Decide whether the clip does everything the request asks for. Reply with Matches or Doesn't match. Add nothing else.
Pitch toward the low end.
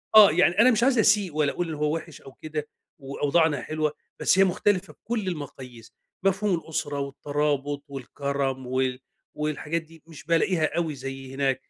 Doesn't match